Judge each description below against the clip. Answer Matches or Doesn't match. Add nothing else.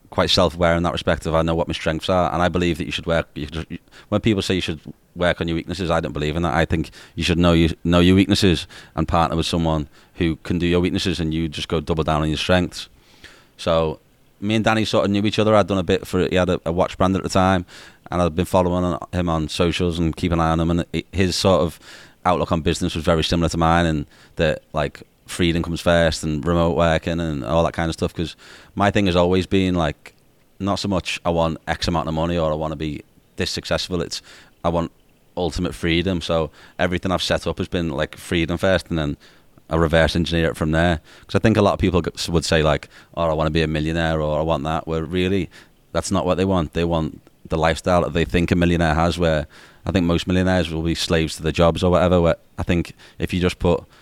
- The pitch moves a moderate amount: Doesn't match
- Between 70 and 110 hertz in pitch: Matches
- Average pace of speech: Doesn't match